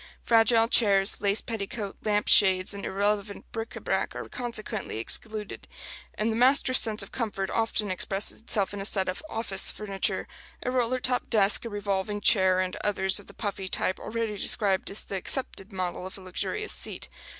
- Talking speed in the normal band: Yes, average, 180 wpm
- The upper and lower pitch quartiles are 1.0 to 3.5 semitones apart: Yes, average, 2.7 semitones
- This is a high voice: Yes, high, 205 Hz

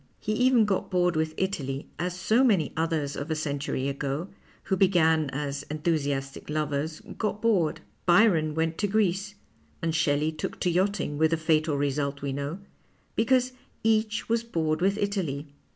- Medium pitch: Yes, medium, 160 Hz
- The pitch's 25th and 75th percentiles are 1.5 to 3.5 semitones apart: No, average, 5.2 semitones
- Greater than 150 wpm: Yes, average, 170 wpm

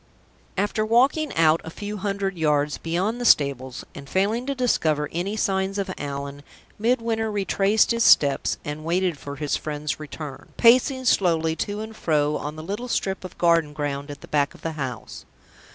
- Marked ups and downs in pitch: Yes, wide, 6.1 semitones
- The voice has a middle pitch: Yes, medium, 170 Hz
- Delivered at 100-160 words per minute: No, average, 175 wpm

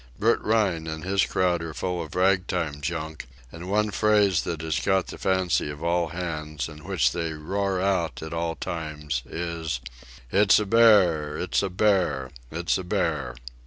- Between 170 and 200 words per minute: Yes, average, 175 wpm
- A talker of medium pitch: No, very low, 85 Hz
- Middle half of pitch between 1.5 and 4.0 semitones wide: Yes, average, 3.4 semitones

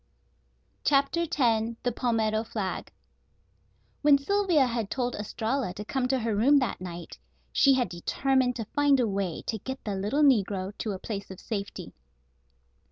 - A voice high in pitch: Yes, high, 230 Hz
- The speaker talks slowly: No, average, 160 wpm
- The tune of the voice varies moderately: Yes, average, 4.8 semitones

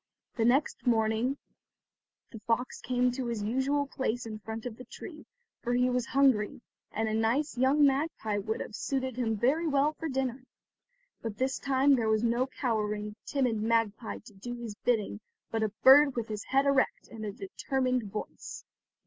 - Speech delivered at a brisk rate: No, average, 175 wpm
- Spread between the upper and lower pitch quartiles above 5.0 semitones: No, average, 3.3 semitones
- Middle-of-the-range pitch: No, high, 245 Hz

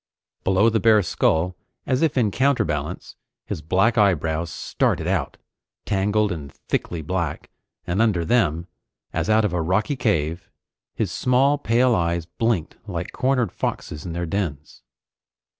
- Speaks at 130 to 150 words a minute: Yes, average, 140 wpm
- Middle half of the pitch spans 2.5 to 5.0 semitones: No, wide, 5.4 semitones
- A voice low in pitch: Yes, very low, 95 Hz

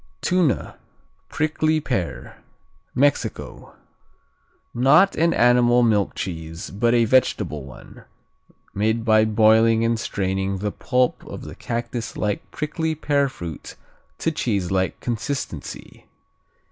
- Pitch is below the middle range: Yes, low, 115 Hz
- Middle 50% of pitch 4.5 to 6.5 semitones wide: Yes, average, 5.2 semitones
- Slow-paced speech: Yes, slow, 105 wpm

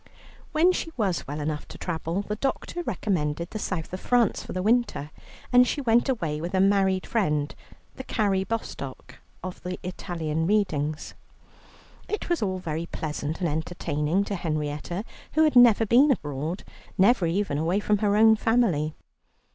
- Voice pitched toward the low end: No, medium, 185 Hz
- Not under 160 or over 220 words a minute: Yes, average, 165 wpm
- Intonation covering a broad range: Yes, wide, 6.0 semitones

